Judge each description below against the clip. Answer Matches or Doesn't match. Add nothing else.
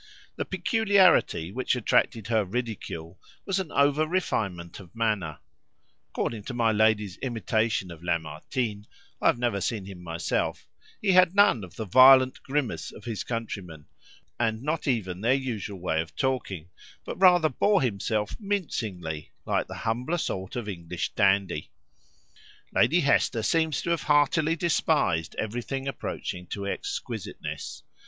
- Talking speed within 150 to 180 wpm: Doesn't match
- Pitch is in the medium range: Doesn't match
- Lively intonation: Matches